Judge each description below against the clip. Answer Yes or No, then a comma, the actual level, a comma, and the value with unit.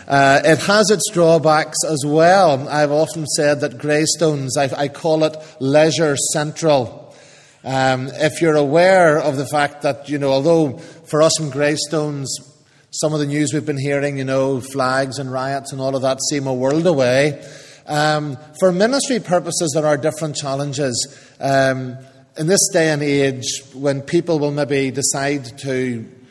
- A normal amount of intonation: No, narrow, 2.3 semitones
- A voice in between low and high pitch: Yes, medium, 145 Hz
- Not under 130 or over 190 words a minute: Yes, average, 165 wpm